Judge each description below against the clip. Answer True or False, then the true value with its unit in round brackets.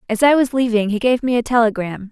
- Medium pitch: False (235 Hz)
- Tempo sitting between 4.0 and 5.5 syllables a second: False (6.2 syllables/s)